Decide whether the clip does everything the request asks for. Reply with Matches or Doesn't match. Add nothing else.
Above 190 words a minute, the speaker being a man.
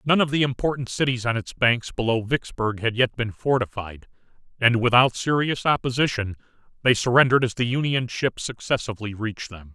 Doesn't match